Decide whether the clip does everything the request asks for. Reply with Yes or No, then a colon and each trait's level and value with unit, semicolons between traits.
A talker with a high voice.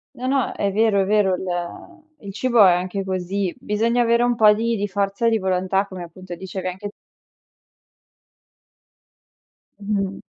Yes: high, 200 Hz